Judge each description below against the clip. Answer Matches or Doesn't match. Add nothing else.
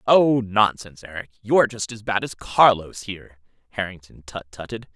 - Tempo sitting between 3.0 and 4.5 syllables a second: Doesn't match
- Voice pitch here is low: Matches